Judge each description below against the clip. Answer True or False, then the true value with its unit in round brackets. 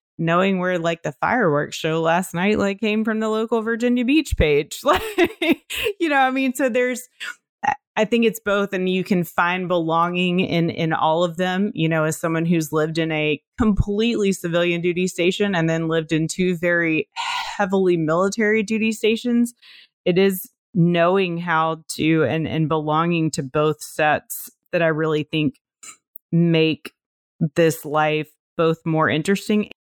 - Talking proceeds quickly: False (160 wpm)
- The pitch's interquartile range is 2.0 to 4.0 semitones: False (5.3 semitones)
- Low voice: False (180 Hz)